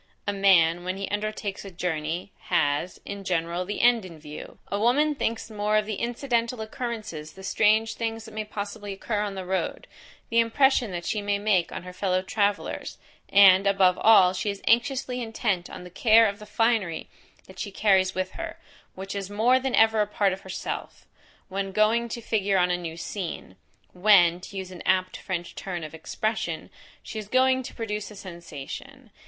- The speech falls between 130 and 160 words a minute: No, average, 190 wpm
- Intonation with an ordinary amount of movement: Yes, average, 3.3 semitones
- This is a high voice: Yes, high, 200 Hz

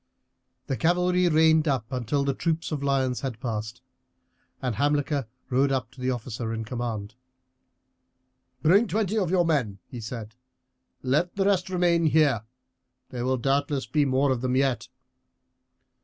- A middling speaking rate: Yes, average, 145 wpm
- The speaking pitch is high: No, low, 135 Hz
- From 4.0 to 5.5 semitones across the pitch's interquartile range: Yes, average, 4.6 semitones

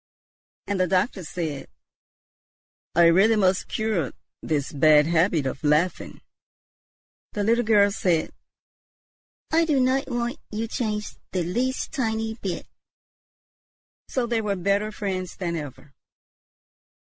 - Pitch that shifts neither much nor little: Yes, average, 4.8 semitones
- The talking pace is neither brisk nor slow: No, slow, 120 wpm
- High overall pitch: Yes, high, 200 Hz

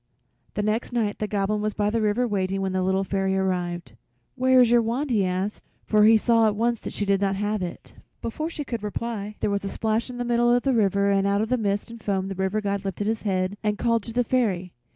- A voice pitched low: No, high, 210 Hz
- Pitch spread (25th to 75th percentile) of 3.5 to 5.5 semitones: No, average, 3.0 semitones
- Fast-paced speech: Yes, fast, 250 wpm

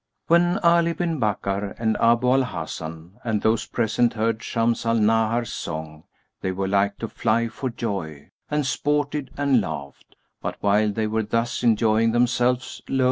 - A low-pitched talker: Yes, low, 115 Hz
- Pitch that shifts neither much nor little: Yes, average, 3.6 semitones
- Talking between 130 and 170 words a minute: Yes, average, 160 wpm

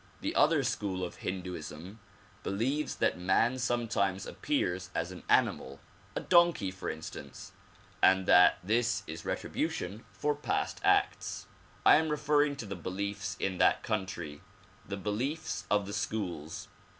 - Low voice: Yes, low, 100 Hz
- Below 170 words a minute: Yes, average, 140 wpm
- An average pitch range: Yes, average, 4.7 semitones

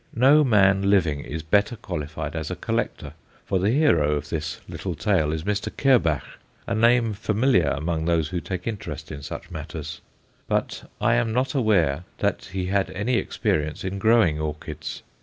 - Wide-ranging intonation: Yes, wide, 6.2 semitones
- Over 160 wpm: Yes, average, 170 wpm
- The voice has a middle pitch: No, very low, 95 Hz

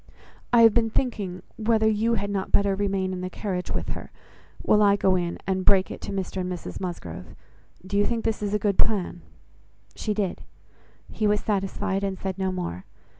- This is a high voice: Yes, high, 195 Hz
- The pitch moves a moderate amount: No, narrow, 2.2 semitones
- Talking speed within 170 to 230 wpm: Yes, average, 200 wpm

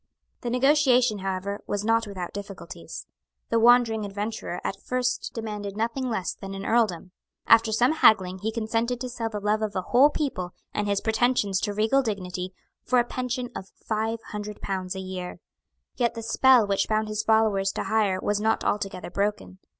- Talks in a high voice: Yes, high, 215 Hz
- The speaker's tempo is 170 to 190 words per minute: Yes, average, 180 wpm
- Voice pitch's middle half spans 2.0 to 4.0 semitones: Yes, average, 3.1 semitones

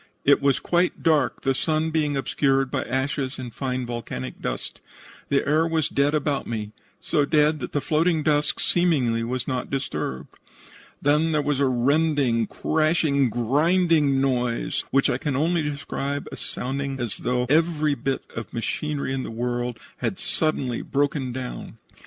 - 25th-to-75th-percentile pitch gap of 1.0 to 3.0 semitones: No, average, 3.4 semitones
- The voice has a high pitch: No, medium, 140 Hz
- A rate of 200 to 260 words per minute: No, average, 160 wpm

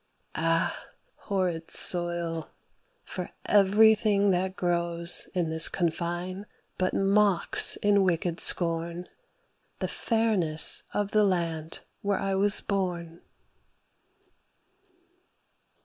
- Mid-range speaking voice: Yes, medium, 180 Hz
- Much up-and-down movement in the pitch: No, average, 2.9 semitones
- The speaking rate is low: Yes, slow, 90 wpm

